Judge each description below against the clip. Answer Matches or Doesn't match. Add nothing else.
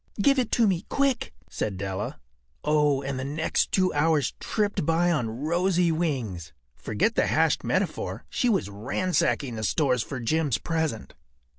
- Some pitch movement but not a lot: Doesn't match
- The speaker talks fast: Doesn't match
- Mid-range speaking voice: Matches